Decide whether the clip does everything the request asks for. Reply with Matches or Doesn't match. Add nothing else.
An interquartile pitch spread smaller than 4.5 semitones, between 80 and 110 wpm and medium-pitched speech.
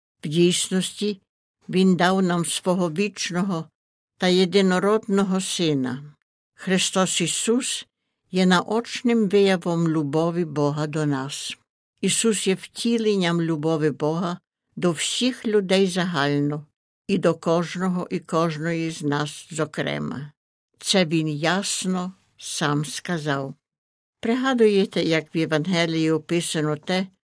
Matches